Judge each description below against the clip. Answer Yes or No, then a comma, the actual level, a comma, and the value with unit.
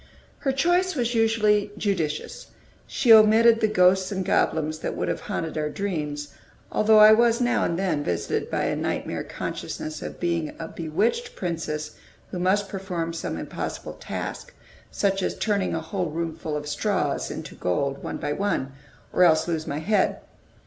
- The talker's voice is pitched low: No, medium, 185 Hz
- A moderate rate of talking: Yes, average, 165 wpm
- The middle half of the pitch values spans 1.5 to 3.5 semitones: No, wide, 5.4 semitones